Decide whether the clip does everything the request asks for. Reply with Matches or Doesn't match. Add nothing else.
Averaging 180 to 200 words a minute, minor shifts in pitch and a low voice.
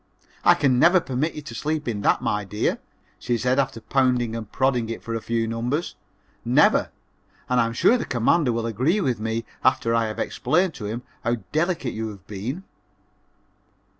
Doesn't match